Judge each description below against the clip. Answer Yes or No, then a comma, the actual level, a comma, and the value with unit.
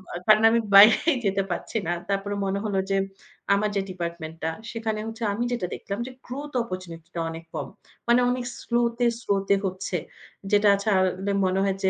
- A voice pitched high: Yes, high, 200 Hz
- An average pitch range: Yes, average, 3.4 semitones